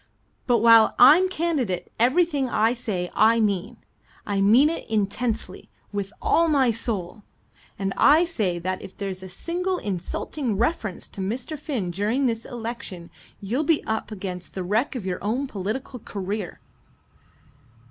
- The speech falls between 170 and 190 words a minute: No, average, 145 wpm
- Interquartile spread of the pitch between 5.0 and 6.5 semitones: Yes, average, 5.3 semitones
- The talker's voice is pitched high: Yes, high, 220 Hz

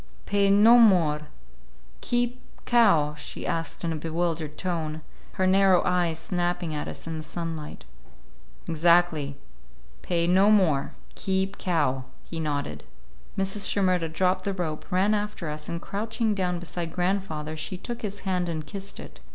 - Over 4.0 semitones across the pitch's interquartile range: No, average, 3.6 semitones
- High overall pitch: No, medium, 175 Hz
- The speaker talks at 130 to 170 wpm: Yes, average, 150 wpm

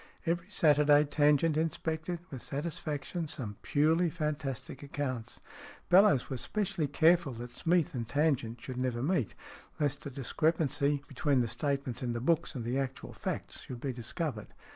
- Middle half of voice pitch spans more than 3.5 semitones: Yes, average, 3.9 semitones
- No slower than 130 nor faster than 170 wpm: Yes, average, 150 wpm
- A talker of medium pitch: Yes, medium, 145 Hz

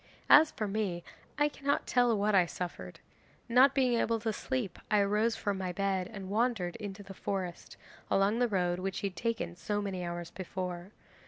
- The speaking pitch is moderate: No, high, 200 Hz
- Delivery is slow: No, average, 185 wpm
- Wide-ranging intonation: No, average, 4.0 semitones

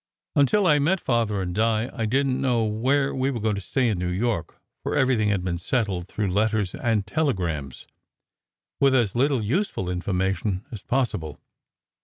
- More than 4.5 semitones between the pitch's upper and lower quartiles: Yes, wide, 5.5 semitones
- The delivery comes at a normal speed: Yes, average, 170 wpm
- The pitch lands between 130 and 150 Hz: No, low, 110 Hz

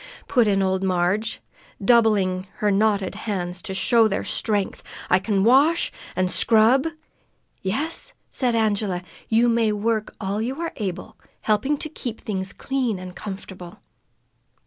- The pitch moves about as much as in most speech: Yes, average, 3.5 semitones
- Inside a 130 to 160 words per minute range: Yes, average, 145 wpm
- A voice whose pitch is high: Yes, high, 210 Hz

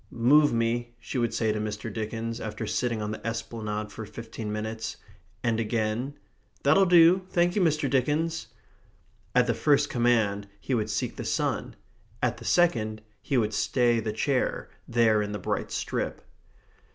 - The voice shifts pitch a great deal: No, average, 4.1 semitones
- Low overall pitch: Yes, low, 115 Hz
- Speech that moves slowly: No, average, 165 wpm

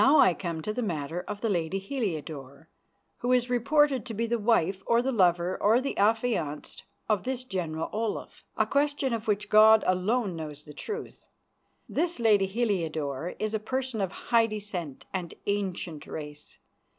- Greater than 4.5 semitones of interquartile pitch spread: Yes, wide, 5.5 semitones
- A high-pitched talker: Yes, high, 205 Hz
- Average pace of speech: Yes, average, 170 wpm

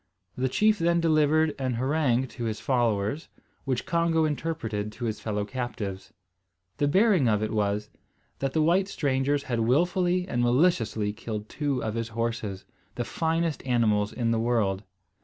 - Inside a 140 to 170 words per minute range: Yes, average, 160 wpm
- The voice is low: Yes, low, 125 Hz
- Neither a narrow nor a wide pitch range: No, wide, 6.1 semitones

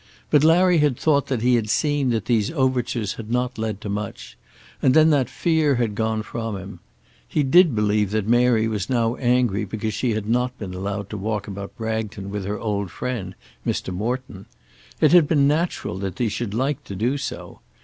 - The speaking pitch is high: No, low, 115 Hz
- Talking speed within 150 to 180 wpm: No, average, 200 wpm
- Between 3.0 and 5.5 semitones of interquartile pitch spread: Yes, average, 4.1 semitones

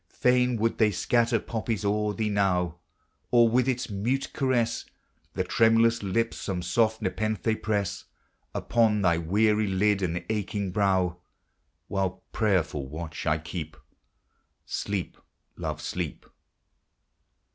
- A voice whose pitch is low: Yes, low, 105 Hz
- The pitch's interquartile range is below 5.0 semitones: Yes, average, 3.6 semitones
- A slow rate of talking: Yes, slow, 120 wpm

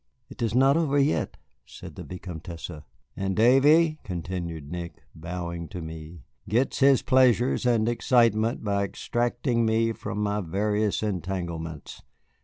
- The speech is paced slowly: Yes, slow, 130 wpm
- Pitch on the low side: Yes, low, 105 Hz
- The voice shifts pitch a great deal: Yes, wide, 5.9 semitones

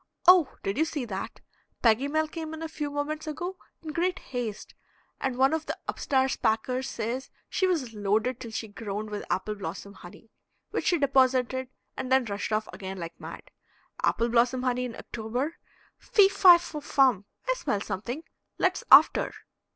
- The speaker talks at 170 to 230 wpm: Yes, average, 175 wpm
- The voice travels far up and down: Yes, wide, 5.8 semitones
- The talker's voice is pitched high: Yes, very high, 255 Hz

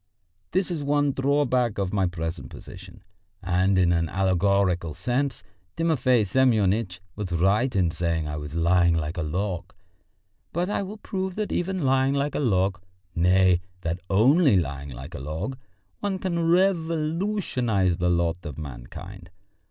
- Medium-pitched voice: No, low, 100 Hz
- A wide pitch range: Yes, wide, 8.7 semitones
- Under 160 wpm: Yes, average, 150 wpm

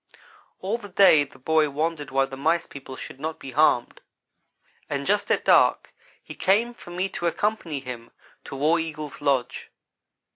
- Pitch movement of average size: Yes, average, 4.2 semitones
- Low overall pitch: No, medium, 155 Hz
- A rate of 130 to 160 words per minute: No, average, 170 wpm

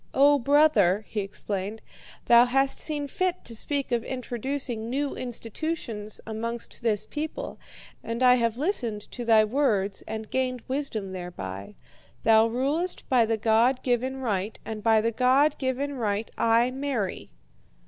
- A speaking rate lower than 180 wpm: Yes, average, 145 wpm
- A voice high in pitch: Yes, high, 235 Hz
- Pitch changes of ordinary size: Yes, average, 3.7 semitones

